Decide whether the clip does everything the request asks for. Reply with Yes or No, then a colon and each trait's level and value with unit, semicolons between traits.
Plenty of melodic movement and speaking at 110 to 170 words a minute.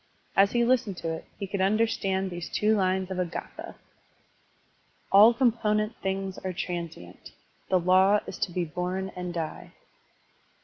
No: average, 2.7 semitones; average, 150 wpm